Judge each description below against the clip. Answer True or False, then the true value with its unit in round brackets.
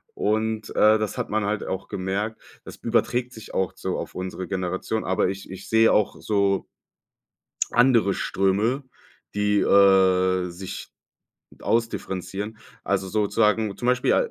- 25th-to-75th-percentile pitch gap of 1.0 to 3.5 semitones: True (2.6 semitones)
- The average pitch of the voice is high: False (105 Hz)